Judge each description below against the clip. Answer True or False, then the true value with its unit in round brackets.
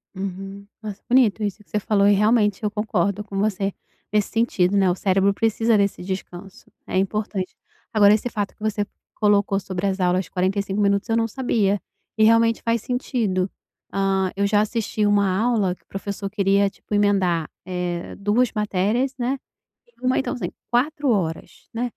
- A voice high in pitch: True (205 Hz)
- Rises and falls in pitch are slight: True (2.2 semitones)